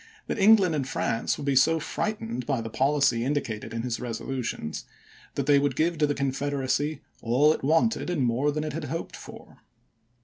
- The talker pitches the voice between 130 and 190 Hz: Yes, medium, 140 Hz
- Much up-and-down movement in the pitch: No, average, 3.5 semitones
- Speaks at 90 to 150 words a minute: No, average, 195 wpm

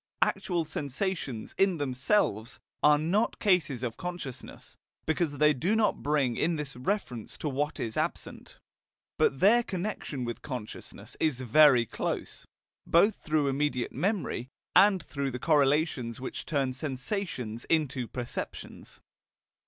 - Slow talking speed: Yes, slow, 130 wpm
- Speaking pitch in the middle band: Yes, medium, 145 Hz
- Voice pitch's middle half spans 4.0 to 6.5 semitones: Yes, average, 5.3 semitones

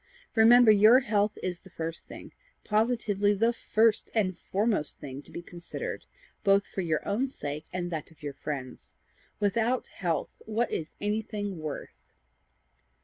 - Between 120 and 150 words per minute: Yes, average, 145 wpm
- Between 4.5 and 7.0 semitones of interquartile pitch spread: Yes, average, 5.1 semitones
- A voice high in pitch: Yes, high, 200 Hz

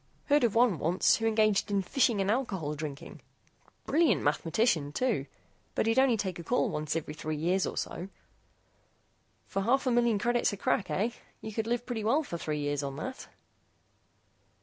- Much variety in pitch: Yes, wide, 7.0 semitones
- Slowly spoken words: No, average, 180 wpm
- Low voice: No, high, 205 Hz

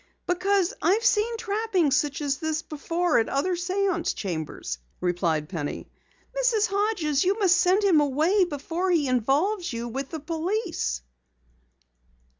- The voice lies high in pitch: Yes, very high, 335 Hz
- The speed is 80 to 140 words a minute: Yes, slow, 135 wpm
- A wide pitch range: Yes, wide, 6.2 semitones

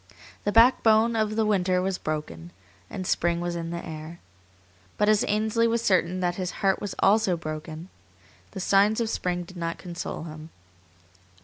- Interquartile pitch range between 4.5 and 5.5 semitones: No, average, 4.0 semitones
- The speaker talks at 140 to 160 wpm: No, average, 170 wpm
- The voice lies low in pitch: No, medium, 185 Hz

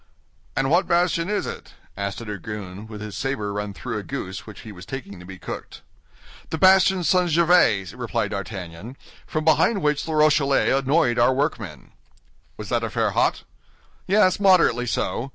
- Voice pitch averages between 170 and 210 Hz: No, low, 130 Hz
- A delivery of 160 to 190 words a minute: Yes, average, 170 wpm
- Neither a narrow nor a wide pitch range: No, wide, 8.2 semitones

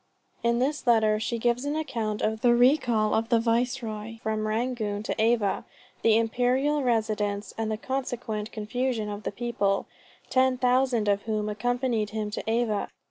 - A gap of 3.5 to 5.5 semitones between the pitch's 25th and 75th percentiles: No, narrow, 2.5 semitones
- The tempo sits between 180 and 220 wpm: No, average, 160 wpm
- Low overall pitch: No, high, 230 Hz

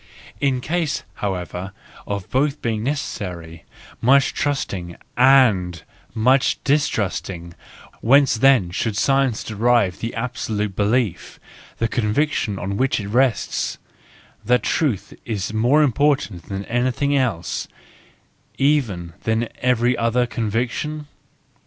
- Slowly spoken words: Yes, slow, 115 wpm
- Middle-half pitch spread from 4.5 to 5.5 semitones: Yes, average, 5.2 semitones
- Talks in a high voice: No, low, 115 Hz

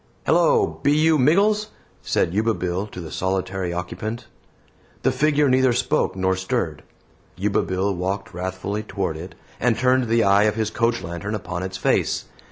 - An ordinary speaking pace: Yes, average, 165 wpm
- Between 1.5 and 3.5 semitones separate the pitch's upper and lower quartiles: No, wide, 5.4 semitones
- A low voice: Yes, low, 105 Hz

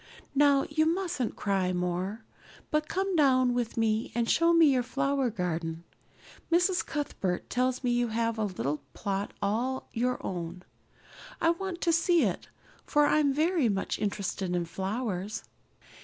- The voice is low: No, high, 245 Hz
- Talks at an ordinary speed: Yes, average, 155 wpm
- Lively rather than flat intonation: Yes, wide, 7.2 semitones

